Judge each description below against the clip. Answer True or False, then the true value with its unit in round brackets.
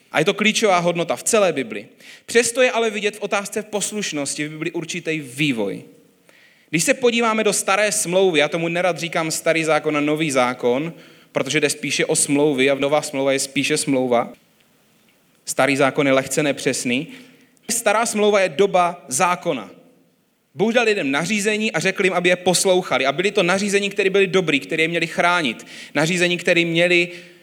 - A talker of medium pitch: True (175 Hz)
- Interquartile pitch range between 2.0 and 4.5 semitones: False (5.2 semitones)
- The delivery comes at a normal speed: False (175 wpm)